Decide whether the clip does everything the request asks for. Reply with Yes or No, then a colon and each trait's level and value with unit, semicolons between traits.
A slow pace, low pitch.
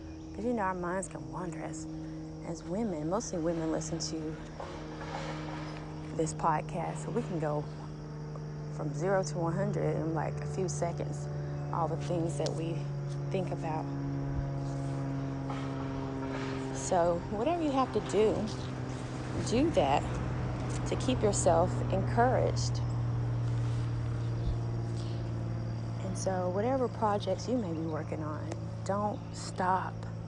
Yes: slow, 115 wpm; low, 120 Hz